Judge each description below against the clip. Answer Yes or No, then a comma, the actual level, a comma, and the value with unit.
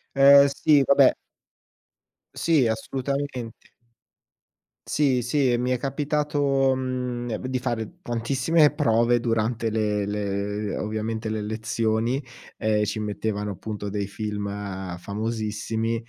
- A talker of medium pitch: No, low, 115 Hz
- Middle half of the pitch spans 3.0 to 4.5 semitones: Yes, average, 3.8 semitones